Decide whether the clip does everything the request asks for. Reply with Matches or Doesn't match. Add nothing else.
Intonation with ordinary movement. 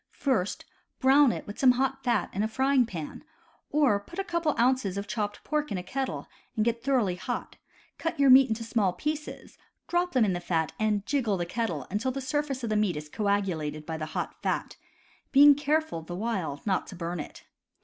Doesn't match